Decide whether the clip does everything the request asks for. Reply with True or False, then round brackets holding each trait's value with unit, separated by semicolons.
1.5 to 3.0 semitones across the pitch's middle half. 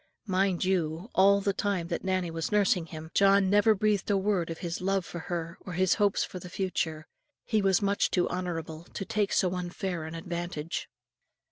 True (2.7 semitones)